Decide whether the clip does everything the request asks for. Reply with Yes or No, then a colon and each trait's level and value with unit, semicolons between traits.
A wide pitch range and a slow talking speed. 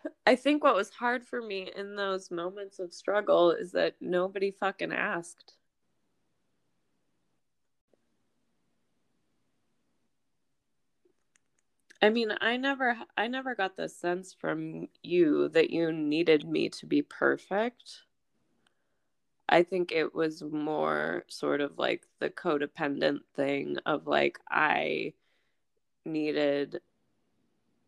Yes: wide, 5.9 semitones; slow, 110 wpm